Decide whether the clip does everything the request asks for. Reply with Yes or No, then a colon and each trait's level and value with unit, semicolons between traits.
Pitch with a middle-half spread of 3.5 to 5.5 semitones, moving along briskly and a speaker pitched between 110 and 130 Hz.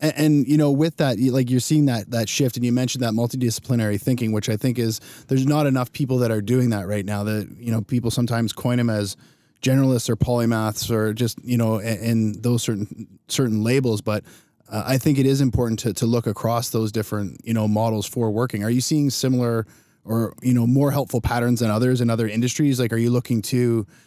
No: narrow, 2.4 semitones; fast, 225 wpm; low, 120 Hz